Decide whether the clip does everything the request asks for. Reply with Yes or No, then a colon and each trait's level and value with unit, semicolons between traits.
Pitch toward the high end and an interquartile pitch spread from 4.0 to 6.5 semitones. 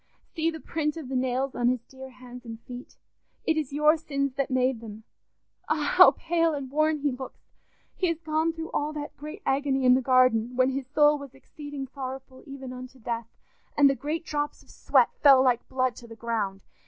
No: very high, 270 Hz; average, 2.8 semitones